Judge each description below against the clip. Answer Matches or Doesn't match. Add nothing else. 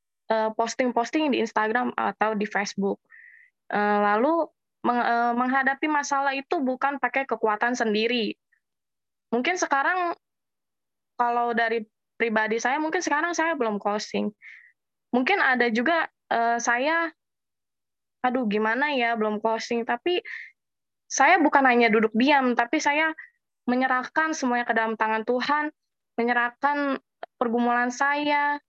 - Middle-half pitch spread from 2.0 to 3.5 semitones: Doesn't match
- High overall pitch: Matches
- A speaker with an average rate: Matches